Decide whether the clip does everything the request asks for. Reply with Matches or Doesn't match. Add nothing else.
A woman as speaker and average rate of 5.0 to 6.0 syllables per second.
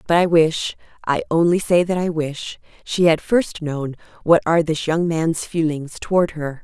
Doesn't match